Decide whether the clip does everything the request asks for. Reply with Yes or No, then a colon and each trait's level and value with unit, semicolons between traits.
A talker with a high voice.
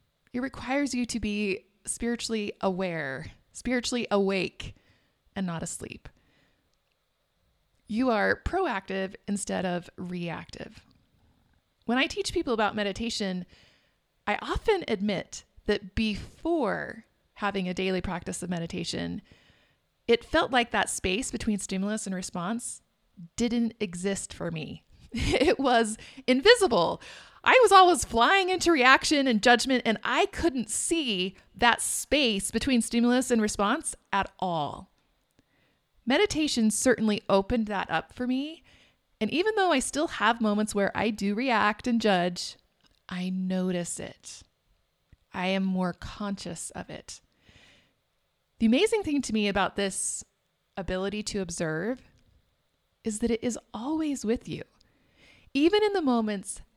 Yes: high, 225 Hz